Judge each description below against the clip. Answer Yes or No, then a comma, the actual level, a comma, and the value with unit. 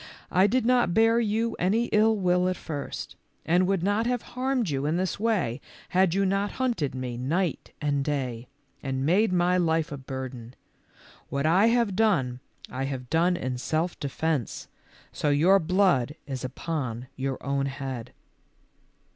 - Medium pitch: Yes, medium, 165 Hz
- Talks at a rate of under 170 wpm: Yes, average, 160 wpm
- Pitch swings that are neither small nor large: No, wide, 6.6 semitones